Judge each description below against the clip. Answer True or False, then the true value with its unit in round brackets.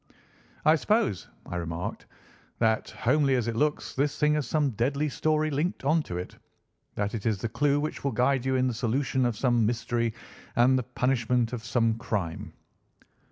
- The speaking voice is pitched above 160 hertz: False (125 Hz)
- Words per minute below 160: False (175 wpm)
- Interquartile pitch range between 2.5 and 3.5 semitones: False (4.0 semitones)